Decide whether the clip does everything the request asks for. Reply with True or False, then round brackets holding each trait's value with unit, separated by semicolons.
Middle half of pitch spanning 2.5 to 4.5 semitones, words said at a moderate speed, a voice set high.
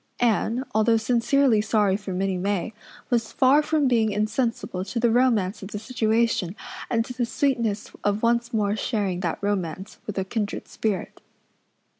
True (2.9 semitones; 160 wpm; 220 Hz)